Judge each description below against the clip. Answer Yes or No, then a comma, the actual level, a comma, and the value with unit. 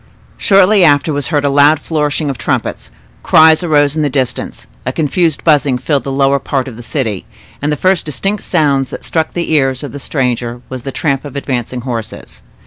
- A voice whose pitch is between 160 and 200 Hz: No, medium, 145 Hz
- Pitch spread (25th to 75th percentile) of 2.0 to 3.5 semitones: Yes, average, 3.0 semitones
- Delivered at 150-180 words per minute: No, average, 200 wpm